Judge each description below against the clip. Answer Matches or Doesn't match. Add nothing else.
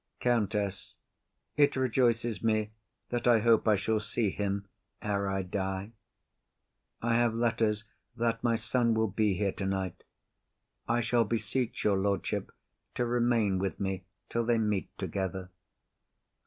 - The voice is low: Matches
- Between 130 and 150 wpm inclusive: Matches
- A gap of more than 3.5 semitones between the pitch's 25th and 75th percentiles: Doesn't match